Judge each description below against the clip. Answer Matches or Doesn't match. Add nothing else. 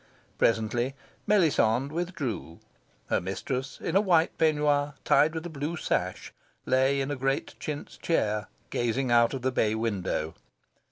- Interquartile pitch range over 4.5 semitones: Matches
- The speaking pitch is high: Doesn't match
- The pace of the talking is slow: Doesn't match